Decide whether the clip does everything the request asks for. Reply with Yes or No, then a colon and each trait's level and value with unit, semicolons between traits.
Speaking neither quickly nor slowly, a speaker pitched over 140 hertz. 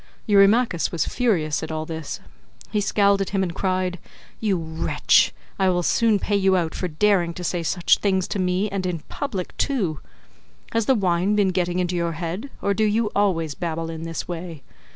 Yes: average, 195 wpm; medium, 185 Hz